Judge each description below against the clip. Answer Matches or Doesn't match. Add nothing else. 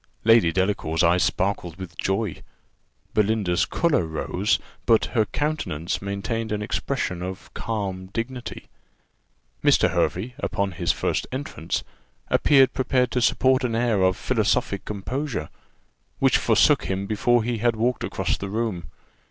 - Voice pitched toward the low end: Matches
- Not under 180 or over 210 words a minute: Doesn't match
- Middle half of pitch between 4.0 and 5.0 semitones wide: Matches